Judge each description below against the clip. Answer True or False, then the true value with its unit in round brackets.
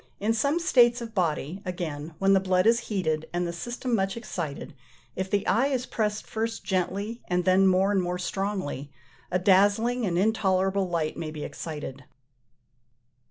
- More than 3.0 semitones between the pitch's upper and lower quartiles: True (4.0 semitones)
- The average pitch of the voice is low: False (190 Hz)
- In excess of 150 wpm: True (165 wpm)